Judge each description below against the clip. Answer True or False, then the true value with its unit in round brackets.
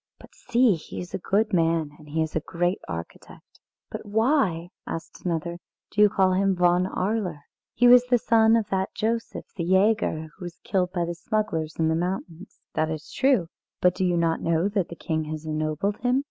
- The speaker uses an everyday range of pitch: True (4.4 semitones)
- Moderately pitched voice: True (180 Hz)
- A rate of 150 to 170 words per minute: False (200 wpm)